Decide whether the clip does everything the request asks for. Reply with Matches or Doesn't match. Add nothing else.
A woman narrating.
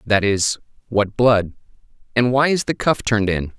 Doesn't match